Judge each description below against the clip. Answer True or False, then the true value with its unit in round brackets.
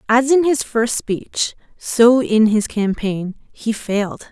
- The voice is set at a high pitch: True (225 Hz)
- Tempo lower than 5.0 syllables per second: True (3.5 syllables/s)